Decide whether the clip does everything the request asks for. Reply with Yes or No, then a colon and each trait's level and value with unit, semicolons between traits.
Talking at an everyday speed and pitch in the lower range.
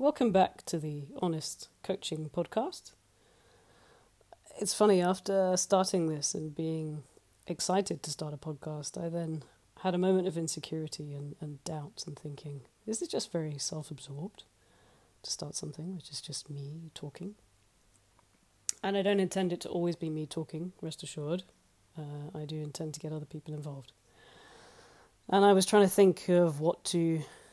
No: average, 160 wpm; medium, 160 Hz